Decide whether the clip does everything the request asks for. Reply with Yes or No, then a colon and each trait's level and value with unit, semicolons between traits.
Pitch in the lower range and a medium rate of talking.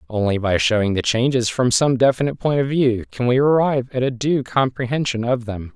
No: low, 125 Hz; fast, 210 wpm